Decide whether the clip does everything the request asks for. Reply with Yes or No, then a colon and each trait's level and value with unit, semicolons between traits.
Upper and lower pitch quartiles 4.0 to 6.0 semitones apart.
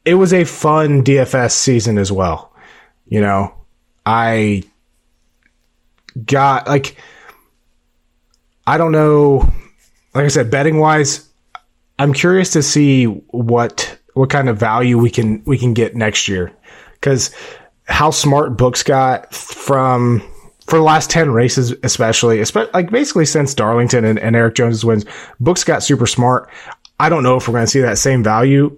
Yes: average, 4.7 semitones